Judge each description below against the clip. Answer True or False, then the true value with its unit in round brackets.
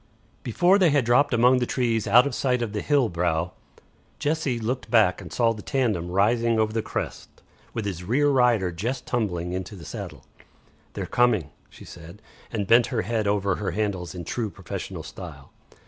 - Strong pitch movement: False (4.7 semitones)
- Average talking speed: True (185 wpm)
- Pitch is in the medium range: False (110 Hz)